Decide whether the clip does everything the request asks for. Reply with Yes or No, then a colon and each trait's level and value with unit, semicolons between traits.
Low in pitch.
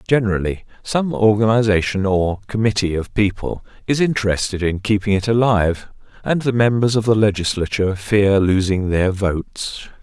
Yes: low, 105 Hz